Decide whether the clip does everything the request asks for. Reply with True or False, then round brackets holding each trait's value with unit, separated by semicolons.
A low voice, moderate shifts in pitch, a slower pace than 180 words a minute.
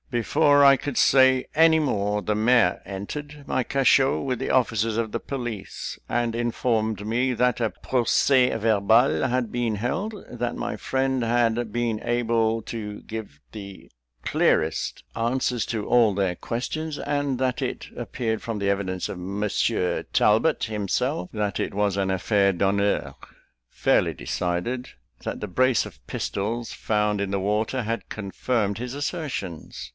True (115 Hz; 3.7 semitones; 145 wpm)